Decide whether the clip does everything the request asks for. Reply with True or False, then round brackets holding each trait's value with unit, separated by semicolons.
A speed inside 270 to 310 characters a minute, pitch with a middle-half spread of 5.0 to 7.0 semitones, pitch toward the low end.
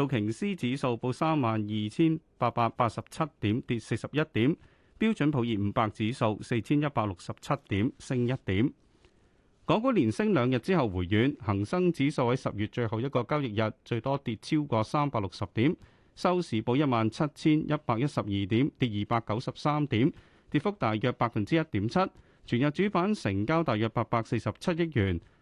True (280 characters per minute; 5.3 semitones; 120 Hz)